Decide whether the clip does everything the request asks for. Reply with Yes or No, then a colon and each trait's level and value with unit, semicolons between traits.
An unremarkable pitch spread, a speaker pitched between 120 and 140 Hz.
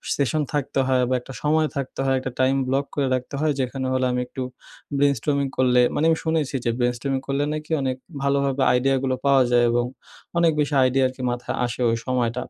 No: narrow, 1.8 semitones; low, 135 Hz